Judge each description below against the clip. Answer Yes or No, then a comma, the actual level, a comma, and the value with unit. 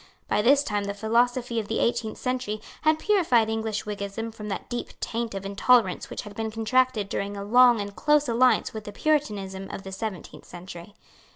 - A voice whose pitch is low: No, high, 220 Hz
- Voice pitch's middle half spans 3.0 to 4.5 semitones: Yes, average, 3.5 semitones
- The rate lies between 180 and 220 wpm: Yes, average, 190 wpm